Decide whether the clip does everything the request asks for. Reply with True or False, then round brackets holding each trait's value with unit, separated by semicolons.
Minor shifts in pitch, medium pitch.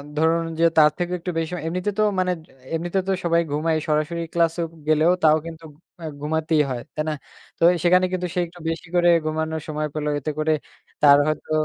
True (2.1 semitones; 160 Hz)